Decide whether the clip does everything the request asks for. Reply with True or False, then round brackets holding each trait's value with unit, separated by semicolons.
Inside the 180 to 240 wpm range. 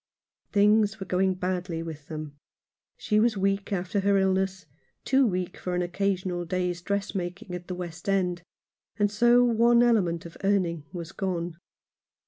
False (155 wpm)